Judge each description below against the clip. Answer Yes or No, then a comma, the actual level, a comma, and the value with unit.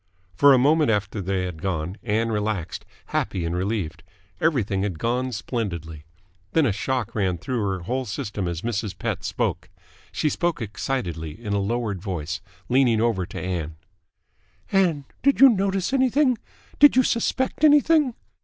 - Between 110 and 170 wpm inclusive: Yes, average, 155 wpm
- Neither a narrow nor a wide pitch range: No, wide, 7.8 semitones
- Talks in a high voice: No, low, 110 Hz